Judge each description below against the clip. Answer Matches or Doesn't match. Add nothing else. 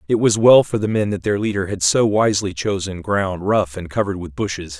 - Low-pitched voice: Matches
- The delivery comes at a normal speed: Doesn't match